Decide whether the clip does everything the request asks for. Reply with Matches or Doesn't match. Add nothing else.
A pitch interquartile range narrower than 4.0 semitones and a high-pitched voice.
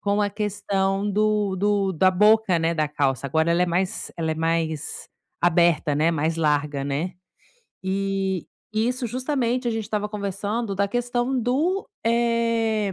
Doesn't match